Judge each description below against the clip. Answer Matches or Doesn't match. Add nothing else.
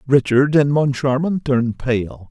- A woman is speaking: Doesn't match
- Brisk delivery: Doesn't match